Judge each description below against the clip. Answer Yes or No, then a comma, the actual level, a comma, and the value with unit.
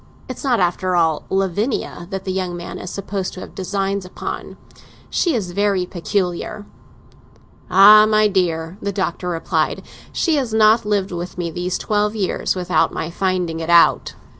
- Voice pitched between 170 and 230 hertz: Yes, high, 190 Hz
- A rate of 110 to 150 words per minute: No, average, 165 wpm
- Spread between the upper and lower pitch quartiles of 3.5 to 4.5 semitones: No, average, 2.8 semitones